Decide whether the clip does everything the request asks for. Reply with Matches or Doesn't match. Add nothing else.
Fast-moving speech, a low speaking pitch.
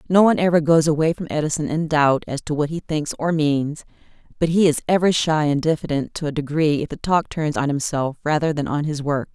Doesn't match